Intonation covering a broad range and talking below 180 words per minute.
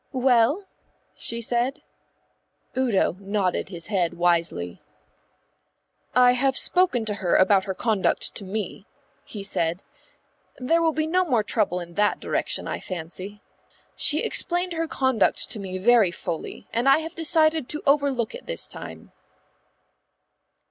Yes: wide, 6.8 semitones; average, 140 wpm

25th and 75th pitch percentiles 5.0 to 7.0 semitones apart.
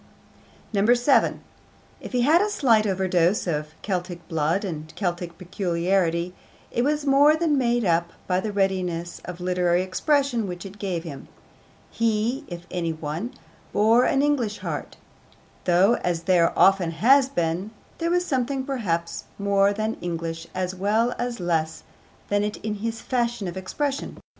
Yes: wide, 5.5 semitones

